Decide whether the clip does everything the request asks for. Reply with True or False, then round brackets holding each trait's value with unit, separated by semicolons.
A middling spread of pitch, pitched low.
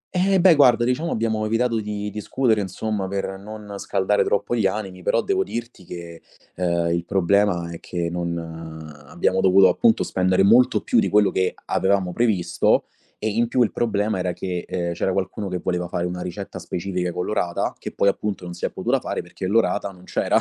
True (3.4 semitones; 100 Hz)